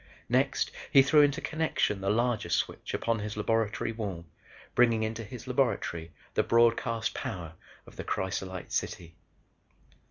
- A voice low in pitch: Yes, low, 115 Hz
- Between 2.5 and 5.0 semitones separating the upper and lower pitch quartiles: Yes, average, 3.9 semitones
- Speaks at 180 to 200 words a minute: No, slow, 135 wpm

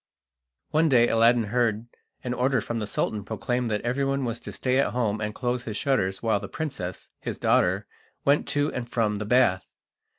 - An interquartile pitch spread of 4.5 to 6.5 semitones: No, average, 3.1 semitones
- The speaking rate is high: No, average, 190 wpm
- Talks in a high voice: No, low, 120 Hz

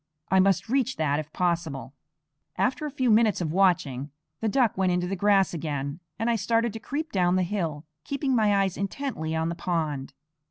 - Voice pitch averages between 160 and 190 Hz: Yes, medium, 185 Hz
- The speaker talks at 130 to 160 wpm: No, average, 195 wpm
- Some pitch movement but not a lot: No, wide, 5.7 semitones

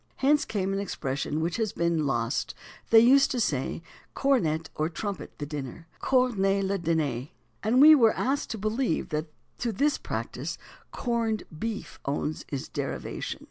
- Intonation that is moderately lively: No, wide, 7.3 semitones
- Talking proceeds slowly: No, average, 155 wpm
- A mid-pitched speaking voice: No, high, 195 Hz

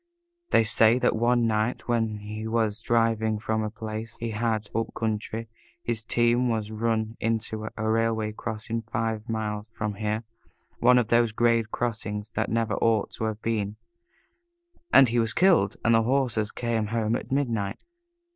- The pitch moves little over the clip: Yes, narrow, 1.3 semitones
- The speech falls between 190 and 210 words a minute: No, average, 165 wpm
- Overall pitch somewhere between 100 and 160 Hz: Yes, low, 110 Hz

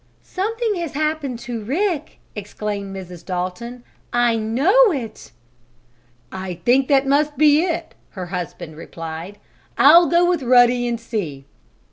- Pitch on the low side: No, high, 245 Hz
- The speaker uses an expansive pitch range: Yes, wide, 7.7 semitones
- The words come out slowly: Yes, slow, 130 wpm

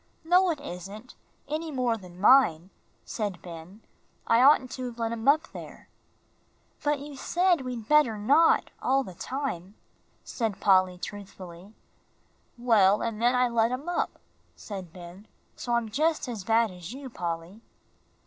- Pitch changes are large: Yes, wide, 6.0 semitones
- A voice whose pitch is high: Yes, high, 230 Hz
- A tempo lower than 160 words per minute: Yes, average, 150 wpm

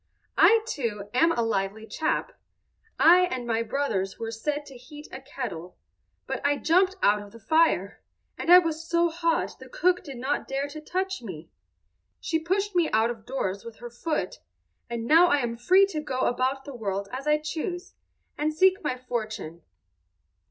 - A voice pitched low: No, very high, 275 Hz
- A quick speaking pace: No, average, 180 wpm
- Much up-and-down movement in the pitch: Yes, wide, 6.5 semitones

